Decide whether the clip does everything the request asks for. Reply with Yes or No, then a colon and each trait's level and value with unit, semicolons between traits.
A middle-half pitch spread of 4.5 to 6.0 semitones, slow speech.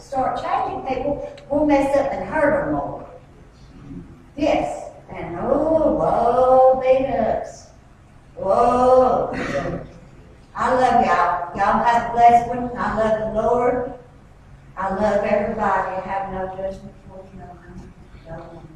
Yes: average, 5.1 semitones; slow, 130 wpm